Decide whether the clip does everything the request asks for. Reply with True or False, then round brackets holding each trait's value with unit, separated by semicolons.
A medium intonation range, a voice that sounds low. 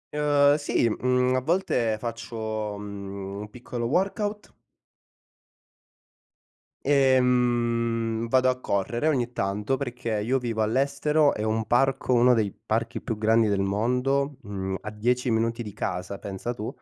True (3.5 semitones; 120 Hz)